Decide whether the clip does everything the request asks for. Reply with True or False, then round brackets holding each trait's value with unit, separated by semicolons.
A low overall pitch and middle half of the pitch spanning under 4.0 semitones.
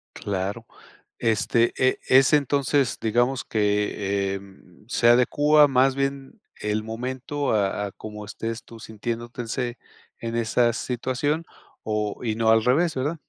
True (120 Hz; 3.6 semitones)